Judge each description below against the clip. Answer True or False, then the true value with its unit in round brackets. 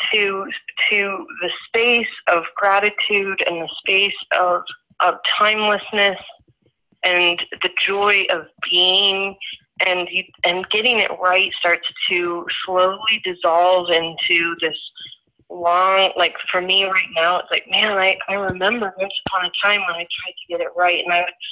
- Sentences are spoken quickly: False (150 wpm)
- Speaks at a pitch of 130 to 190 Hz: True (185 Hz)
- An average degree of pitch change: False (2.3 semitones)